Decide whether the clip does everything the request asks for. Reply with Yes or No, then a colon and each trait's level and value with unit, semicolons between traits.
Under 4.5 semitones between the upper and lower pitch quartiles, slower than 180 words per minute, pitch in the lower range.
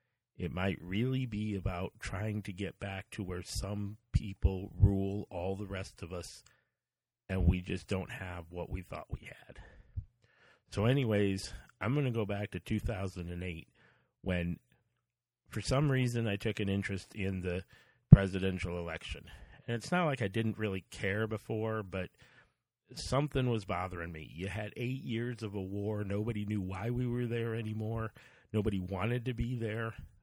Yes: average, 3.5 semitones; average, 165 wpm; low, 105 Hz